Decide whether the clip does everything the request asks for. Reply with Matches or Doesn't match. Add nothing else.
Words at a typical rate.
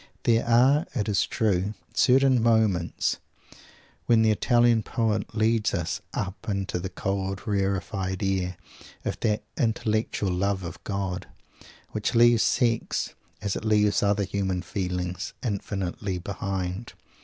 Doesn't match